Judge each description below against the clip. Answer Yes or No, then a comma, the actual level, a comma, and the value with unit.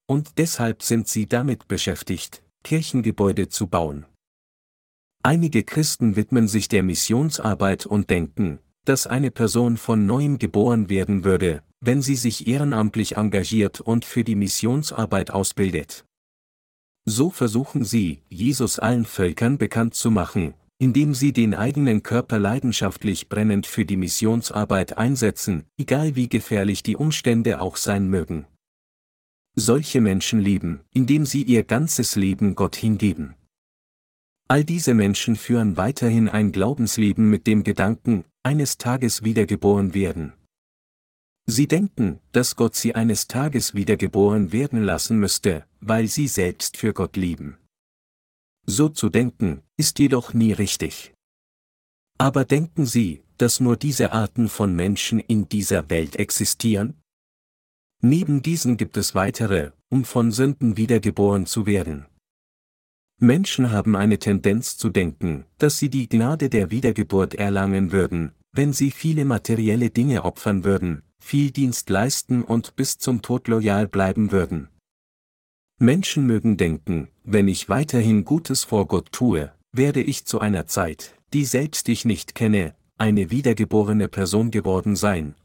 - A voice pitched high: No, low, 110 Hz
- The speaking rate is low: No, average, 135 wpm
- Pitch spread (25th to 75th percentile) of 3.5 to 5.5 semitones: Yes, average, 4.0 semitones